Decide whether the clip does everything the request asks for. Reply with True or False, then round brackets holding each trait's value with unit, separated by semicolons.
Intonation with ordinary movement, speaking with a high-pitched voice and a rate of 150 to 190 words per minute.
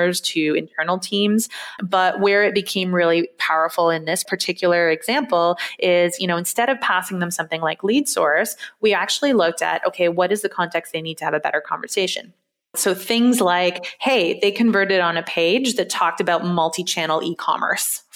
False (3.2 semitones; 180 Hz; 185 wpm)